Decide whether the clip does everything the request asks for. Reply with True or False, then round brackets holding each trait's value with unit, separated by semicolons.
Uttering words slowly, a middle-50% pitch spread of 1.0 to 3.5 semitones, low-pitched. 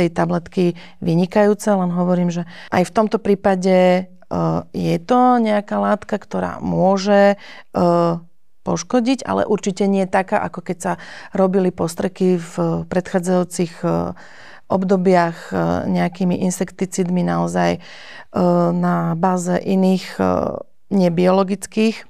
False (100 wpm; 2.5 semitones; 185 Hz)